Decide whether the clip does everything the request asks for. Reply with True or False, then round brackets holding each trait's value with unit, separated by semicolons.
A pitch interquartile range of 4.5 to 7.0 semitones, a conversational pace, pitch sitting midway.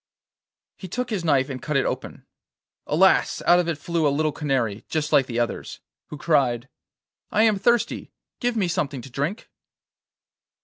True (5.4 semitones; 170 wpm; 150 Hz)